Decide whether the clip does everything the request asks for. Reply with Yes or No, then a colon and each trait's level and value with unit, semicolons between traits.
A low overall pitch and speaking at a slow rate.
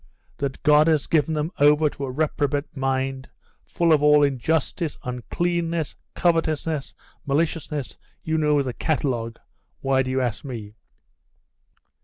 No: medium, 145 Hz; slow, 130 wpm